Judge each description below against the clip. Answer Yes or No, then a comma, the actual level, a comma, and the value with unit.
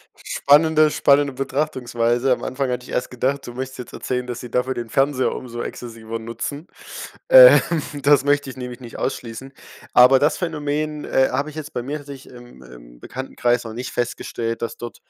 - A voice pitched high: No, low, 130 Hz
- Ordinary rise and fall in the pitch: Yes, average, 3.0 semitones